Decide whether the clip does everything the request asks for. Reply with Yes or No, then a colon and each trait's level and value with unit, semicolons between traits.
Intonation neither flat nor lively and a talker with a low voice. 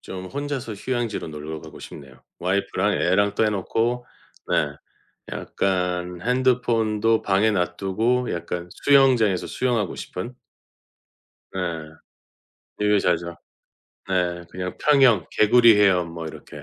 Yes: average, 5.0 semitones; low, 100 Hz